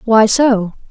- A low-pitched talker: No, high, 225 Hz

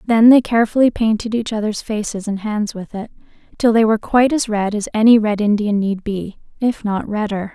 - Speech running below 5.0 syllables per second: No, 5.5 syllables/s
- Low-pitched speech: No, high, 215 Hz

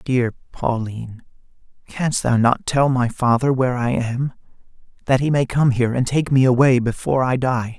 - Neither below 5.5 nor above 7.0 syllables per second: No, 5.0 syllables/s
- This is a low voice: Yes, low, 125 Hz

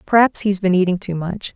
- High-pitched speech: Yes, high, 195 Hz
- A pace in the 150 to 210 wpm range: No, fast, 230 wpm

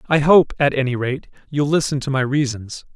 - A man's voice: Yes, male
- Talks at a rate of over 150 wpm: Yes, fast, 205 wpm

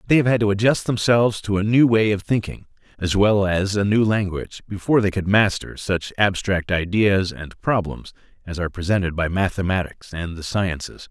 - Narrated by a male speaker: Yes, male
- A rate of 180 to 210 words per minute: Yes, average, 190 wpm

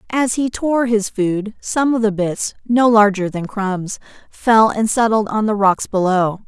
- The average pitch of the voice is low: No, high, 215 Hz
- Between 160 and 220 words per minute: Yes, average, 185 wpm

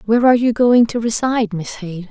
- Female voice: Yes, female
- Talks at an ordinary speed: No, fast, 230 wpm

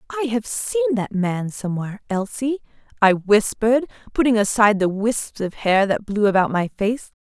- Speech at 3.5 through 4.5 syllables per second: No, 4.9 syllables/s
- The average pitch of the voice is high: Yes, high, 220 Hz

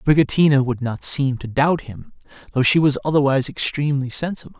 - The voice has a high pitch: No, medium, 140 Hz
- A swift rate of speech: No, average, 170 wpm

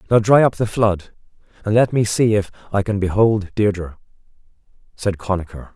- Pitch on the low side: Yes, low, 105 Hz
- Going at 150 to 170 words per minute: Yes, average, 165 wpm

